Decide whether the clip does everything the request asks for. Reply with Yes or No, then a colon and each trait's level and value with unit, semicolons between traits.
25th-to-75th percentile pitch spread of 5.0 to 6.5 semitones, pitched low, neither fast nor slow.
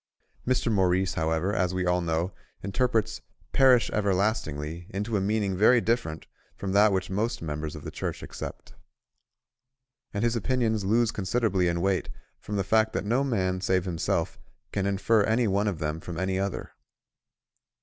No: average, 3.5 semitones; low, 100 Hz; average, 160 wpm